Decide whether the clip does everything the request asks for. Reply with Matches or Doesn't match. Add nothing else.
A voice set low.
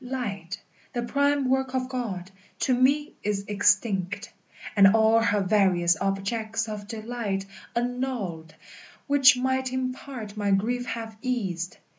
Doesn't match